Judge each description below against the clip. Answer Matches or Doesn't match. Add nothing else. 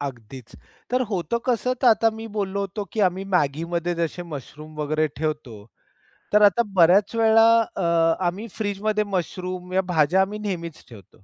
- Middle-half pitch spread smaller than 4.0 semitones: Doesn't match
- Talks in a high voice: Doesn't match